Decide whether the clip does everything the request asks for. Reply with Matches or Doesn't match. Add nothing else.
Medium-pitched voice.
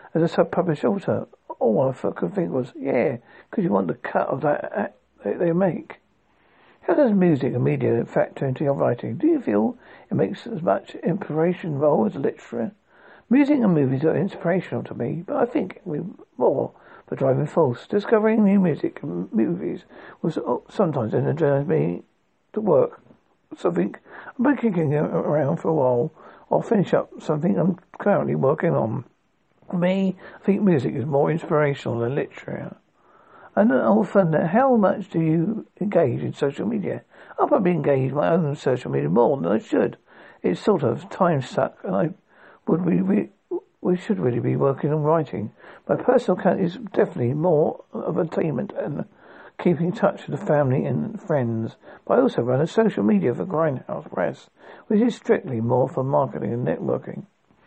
Matches